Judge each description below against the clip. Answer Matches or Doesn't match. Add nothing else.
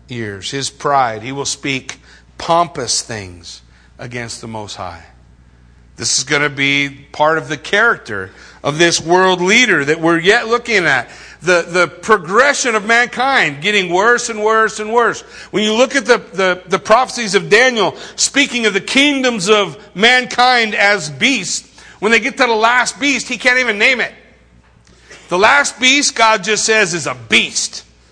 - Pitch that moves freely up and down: Matches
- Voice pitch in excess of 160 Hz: Matches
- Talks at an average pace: Matches